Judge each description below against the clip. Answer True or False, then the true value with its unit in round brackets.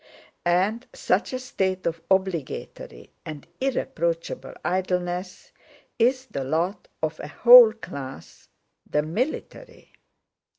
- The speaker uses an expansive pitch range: True (6.3 semitones)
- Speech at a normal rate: False (95 wpm)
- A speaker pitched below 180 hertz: False (185 Hz)